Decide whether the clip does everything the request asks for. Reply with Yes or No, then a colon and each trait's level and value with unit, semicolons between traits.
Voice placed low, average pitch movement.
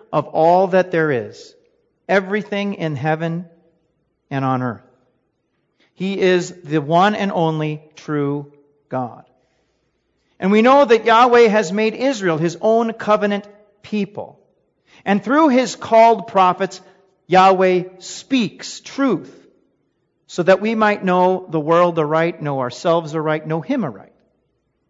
No: medium, 185 Hz; average, 4.9 semitones